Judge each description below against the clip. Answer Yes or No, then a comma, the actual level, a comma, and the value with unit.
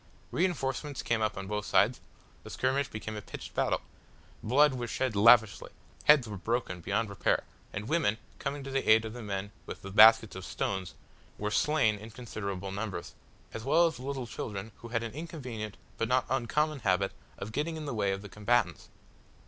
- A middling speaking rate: Yes, average, 190 wpm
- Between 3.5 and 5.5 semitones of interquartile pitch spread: Yes, average, 4.5 semitones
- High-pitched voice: No, low, 115 Hz